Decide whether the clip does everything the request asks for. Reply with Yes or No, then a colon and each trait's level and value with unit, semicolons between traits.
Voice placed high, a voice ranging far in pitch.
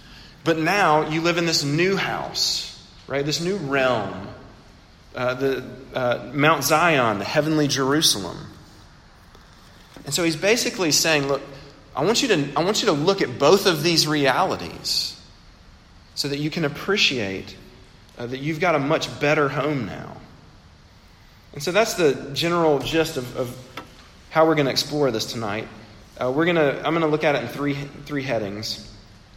No: medium, 140 Hz; wide, 5.8 semitones